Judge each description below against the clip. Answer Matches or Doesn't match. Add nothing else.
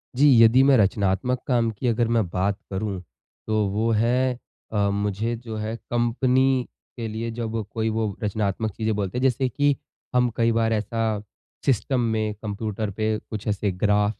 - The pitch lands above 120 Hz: Doesn't match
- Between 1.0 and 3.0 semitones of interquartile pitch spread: Matches